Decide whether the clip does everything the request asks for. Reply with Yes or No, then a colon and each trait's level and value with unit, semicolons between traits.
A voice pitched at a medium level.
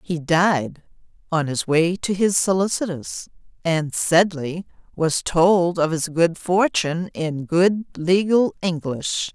Yes: medium, 170 Hz